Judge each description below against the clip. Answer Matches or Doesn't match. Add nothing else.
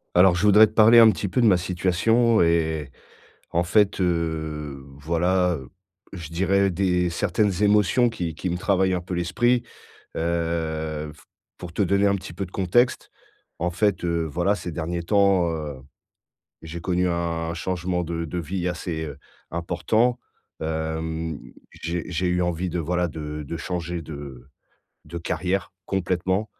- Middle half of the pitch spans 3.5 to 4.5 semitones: Doesn't match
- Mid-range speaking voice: Doesn't match